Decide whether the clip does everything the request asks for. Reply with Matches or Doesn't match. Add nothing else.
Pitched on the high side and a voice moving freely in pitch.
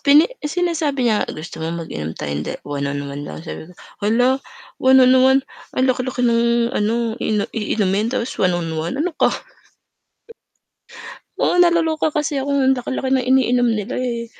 Matches